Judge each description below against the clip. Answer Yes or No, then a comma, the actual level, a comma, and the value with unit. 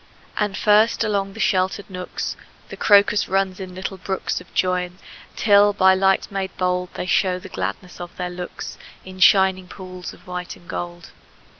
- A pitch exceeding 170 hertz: Yes, medium, 185 Hz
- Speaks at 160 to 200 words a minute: Yes, average, 170 wpm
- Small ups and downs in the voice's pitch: Yes, narrow, 1.3 semitones